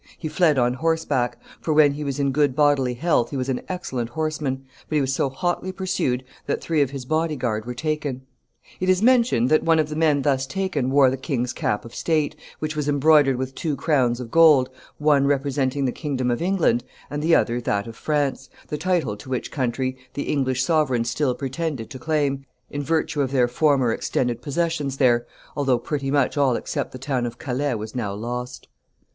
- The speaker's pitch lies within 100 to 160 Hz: Yes, medium, 140 Hz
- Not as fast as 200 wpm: No, fast, 205 wpm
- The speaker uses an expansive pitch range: No, average, 3.4 semitones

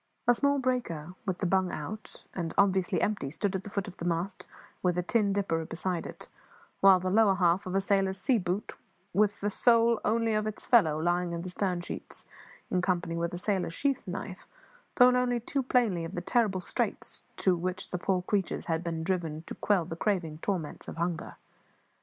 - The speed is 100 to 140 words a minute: No, average, 200 wpm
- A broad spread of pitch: No, average, 3.2 semitones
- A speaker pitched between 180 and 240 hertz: Yes, medium, 185 Hz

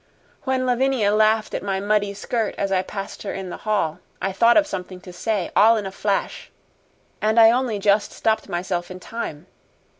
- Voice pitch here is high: Yes, high, 205 Hz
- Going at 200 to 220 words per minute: No, average, 190 wpm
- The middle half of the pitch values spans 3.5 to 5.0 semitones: No, average, 2.8 semitones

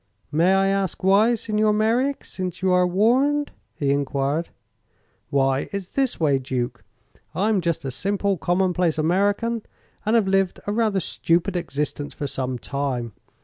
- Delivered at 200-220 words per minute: No, average, 150 wpm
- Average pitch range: No, wide, 6.3 semitones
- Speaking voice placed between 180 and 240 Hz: Yes, medium, 185 Hz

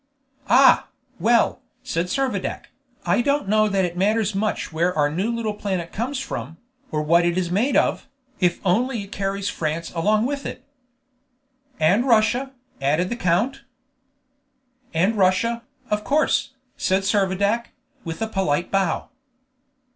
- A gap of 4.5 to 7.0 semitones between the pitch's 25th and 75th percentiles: Yes, average, 4.9 semitones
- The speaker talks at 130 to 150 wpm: Yes, average, 140 wpm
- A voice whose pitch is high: Yes, high, 200 Hz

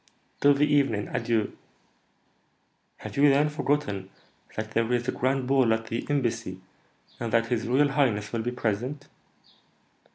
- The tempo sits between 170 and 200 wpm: No, average, 150 wpm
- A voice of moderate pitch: No, low, 120 Hz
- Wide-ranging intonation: No, average, 3.9 semitones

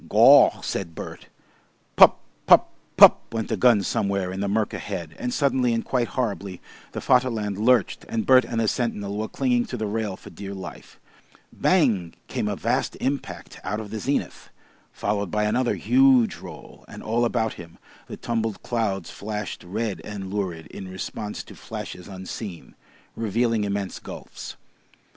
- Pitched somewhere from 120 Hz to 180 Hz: No, low, 105 Hz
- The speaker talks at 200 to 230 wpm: No, average, 160 wpm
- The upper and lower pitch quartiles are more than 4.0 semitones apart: No, average, 3.3 semitones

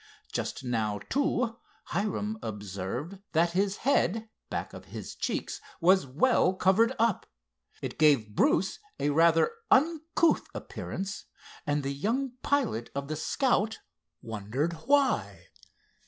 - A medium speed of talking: No, slow, 120 wpm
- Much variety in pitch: Yes, wide, 8.7 semitones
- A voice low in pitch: No, medium, 185 Hz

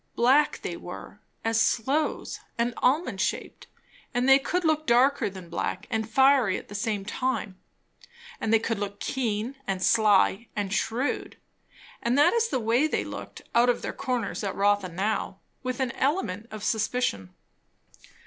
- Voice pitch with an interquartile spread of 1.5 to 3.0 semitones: No, average, 4.3 semitones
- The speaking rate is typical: Yes, average, 160 wpm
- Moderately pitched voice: No, high, 230 Hz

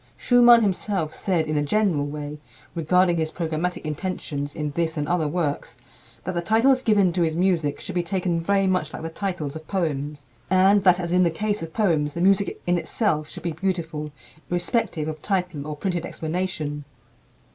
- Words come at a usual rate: Yes, average, 185 wpm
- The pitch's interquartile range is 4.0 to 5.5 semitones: No, average, 3.5 semitones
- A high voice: No, medium, 170 Hz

